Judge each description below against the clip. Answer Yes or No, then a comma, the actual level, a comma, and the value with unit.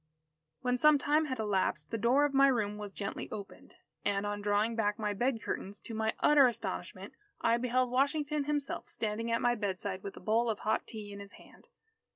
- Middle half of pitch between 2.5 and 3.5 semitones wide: No, average, 4.1 semitones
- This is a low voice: No, high, 225 Hz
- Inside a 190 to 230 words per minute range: Yes, average, 200 wpm